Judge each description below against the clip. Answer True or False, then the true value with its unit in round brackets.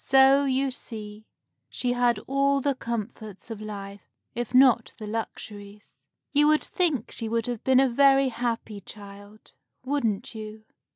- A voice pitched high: True (235 Hz)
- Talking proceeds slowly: False (150 wpm)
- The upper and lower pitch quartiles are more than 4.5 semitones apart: False (4.0 semitones)